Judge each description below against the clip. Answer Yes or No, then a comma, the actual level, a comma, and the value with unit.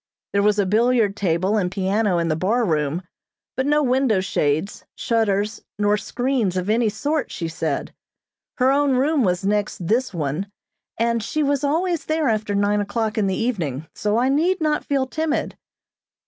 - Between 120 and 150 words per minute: No, average, 175 wpm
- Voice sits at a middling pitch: No, high, 215 Hz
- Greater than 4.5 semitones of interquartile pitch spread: Yes, average, 5.3 semitones